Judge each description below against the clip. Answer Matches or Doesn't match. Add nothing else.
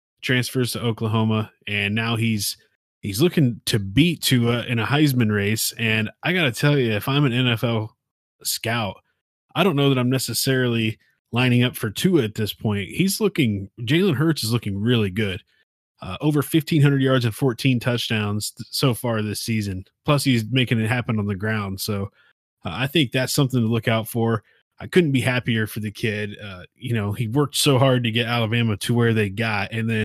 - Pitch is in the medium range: Doesn't match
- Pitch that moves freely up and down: Doesn't match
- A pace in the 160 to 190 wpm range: Doesn't match